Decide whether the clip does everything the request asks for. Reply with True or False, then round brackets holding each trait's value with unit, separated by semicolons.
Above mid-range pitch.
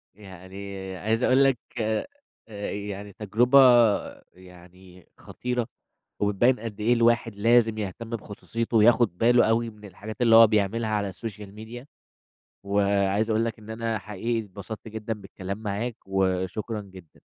False (110 Hz)